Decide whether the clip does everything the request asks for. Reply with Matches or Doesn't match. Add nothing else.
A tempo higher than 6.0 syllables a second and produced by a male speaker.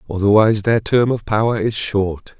Doesn't match